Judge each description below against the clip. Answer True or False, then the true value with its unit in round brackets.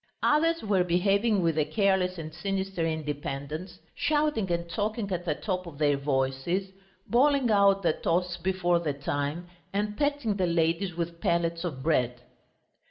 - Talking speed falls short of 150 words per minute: False (155 wpm)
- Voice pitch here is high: False (175 Hz)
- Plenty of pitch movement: False (3.8 semitones)